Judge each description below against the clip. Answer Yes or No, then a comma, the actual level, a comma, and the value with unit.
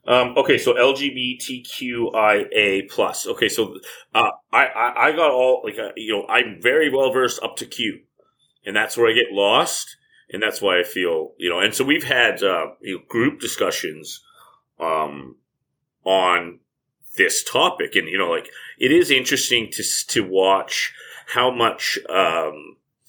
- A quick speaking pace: No, average, 165 wpm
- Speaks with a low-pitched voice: No, medium, 145 Hz